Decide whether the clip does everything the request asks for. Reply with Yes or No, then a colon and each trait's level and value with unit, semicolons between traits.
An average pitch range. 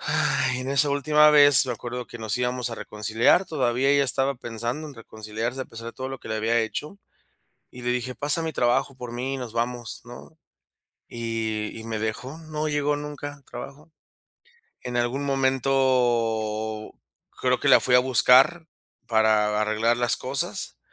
Yes: average, 3.4 semitones